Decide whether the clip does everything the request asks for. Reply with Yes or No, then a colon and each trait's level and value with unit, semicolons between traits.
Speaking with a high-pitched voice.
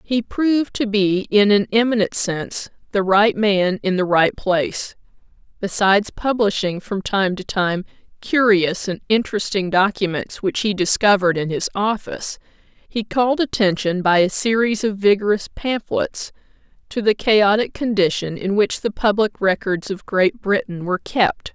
Yes: high, 200 Hz